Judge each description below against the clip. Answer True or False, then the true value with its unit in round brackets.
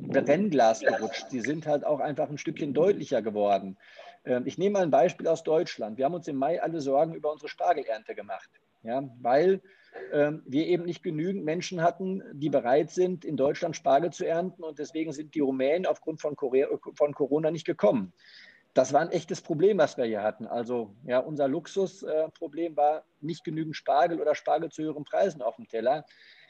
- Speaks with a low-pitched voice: False (155 Hz)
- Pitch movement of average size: True (3.4 semitones)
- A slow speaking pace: False (180 wpm)